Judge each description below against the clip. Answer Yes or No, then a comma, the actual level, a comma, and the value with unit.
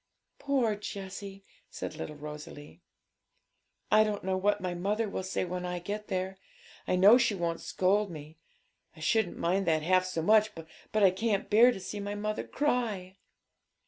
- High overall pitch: Yes, high, 195 Hz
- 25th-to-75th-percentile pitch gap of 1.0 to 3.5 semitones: Yes, average, 2.9 semitones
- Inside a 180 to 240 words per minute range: No, average, 170 wpm